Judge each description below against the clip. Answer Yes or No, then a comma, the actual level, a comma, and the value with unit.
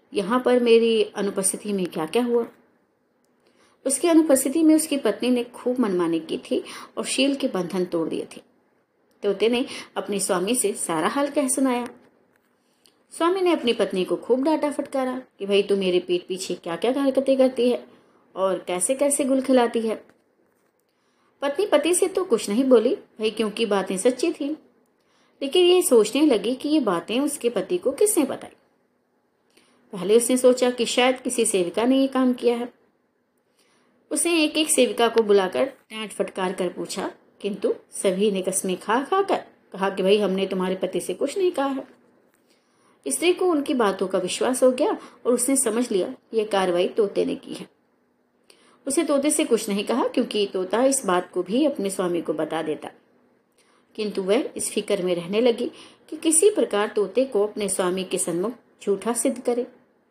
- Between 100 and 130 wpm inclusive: No, average, 175 wpm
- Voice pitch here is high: Yes, high, 235 Hz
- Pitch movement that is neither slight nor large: No, wide, 5.7 semitones